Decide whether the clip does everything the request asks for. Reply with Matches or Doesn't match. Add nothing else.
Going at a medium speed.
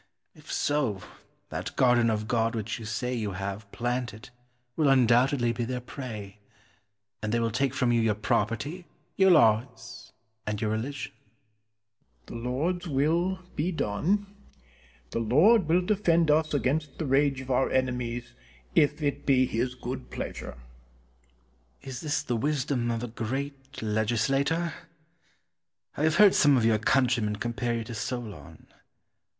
Matches